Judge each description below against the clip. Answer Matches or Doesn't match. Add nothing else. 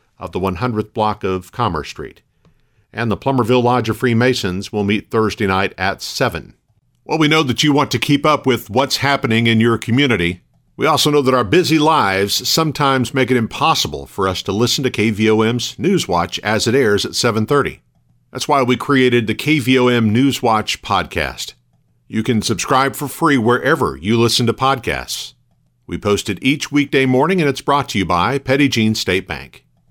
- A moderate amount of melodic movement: Matches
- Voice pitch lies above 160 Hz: Doesn't match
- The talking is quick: Doesn't match